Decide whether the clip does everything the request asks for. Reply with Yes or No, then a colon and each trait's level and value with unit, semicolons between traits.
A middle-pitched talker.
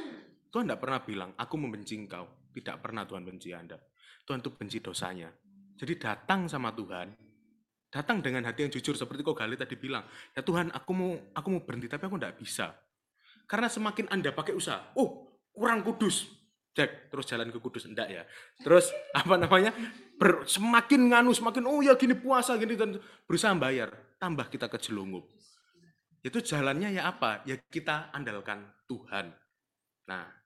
Yes: medium, 150 Hz